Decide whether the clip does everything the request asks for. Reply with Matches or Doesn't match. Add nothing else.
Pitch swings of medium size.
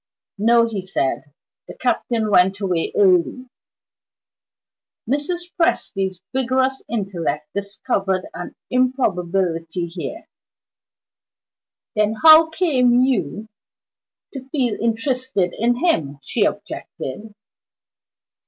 Doesn't match